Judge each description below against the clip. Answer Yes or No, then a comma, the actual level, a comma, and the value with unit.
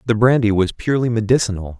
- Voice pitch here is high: No, low, 110 Hz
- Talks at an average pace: Yes, average, 165 wpm